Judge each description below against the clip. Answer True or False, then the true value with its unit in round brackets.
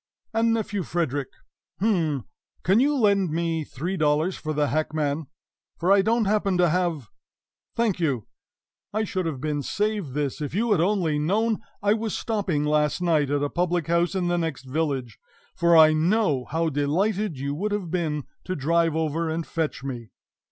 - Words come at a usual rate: True (175 wpm)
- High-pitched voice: False (165 Hz)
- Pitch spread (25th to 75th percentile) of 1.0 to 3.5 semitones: False (4.8 semitones)